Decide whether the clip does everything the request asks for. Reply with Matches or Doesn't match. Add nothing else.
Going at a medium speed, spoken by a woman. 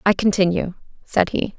Matches